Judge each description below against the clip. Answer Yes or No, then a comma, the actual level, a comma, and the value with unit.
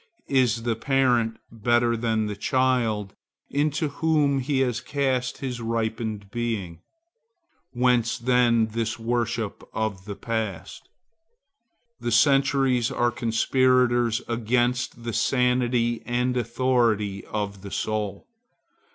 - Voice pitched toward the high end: No, low, 120 Hz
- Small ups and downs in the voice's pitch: Yes, narrow, 2.3 semitones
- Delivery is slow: Yes, slow, 110 wpm